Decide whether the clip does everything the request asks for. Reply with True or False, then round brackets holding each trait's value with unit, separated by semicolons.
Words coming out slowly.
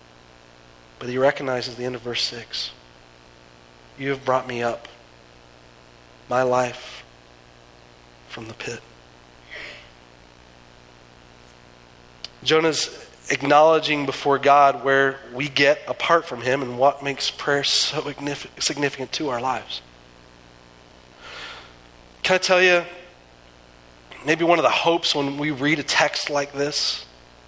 True (115 wpm)